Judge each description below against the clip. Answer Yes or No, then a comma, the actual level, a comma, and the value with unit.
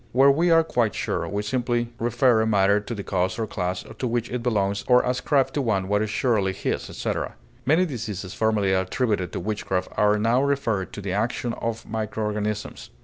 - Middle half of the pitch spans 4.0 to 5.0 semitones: No, average, 3.3 semitones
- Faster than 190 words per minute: Yes, average, 200 wpm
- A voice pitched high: No, low, 110 Hz